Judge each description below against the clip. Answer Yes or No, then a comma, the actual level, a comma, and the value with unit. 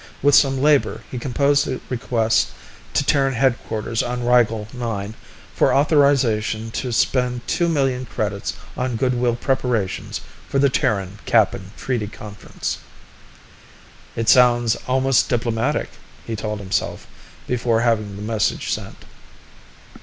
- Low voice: Yes, low, 120 Hz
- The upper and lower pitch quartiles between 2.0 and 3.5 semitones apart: Yes, average, 3.1 semitones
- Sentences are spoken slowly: Yes, slow, 125 wpm